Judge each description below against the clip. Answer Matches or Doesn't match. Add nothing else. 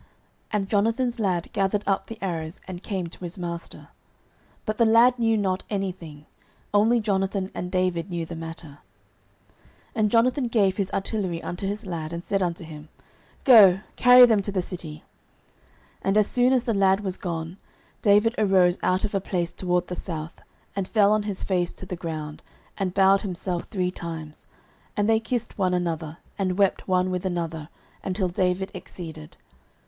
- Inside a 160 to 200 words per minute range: Matches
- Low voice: Doesn't match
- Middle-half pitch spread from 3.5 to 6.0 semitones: Doesn't match